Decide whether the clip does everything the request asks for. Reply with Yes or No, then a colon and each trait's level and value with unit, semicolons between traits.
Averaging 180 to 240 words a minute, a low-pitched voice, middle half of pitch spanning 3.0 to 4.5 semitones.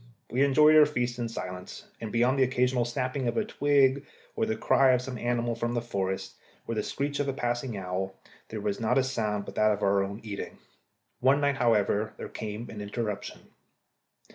Yes: average, 200 wpm; low, 120 Hz; average, 4.1 semitones